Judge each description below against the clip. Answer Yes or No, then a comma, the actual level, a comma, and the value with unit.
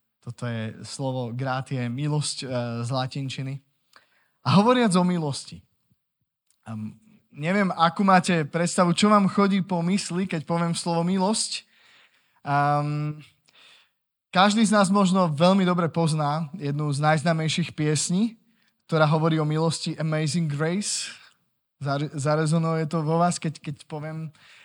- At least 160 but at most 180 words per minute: No, average, 125 wpm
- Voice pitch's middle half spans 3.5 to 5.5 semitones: Yes, average, 3.9 semitones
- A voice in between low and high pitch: Yes, medium, 160 Hz